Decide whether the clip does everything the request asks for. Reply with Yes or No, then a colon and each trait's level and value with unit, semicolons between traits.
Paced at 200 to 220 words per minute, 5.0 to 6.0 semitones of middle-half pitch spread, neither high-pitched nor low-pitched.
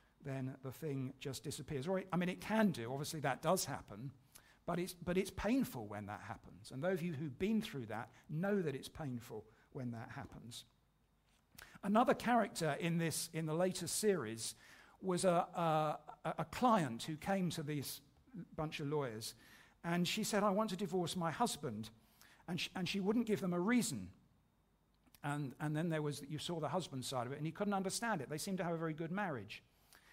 Yes: fast, 205 wpm; wide, 5.6 semitones; medium, 160 Hz